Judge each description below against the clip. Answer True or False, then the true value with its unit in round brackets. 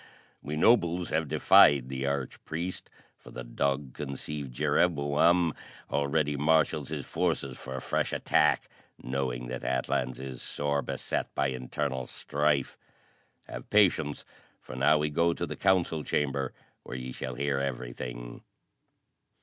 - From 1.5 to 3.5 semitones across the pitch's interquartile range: True (3.0 semitones)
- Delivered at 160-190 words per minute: False (135 wpm)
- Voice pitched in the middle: False (70 Hz)